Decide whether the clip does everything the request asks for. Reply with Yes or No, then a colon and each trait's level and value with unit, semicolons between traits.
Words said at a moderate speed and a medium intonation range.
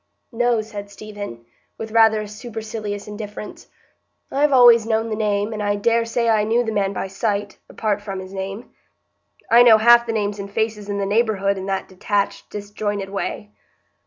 No: average, 175 wpm; narrow, 1.9 semitones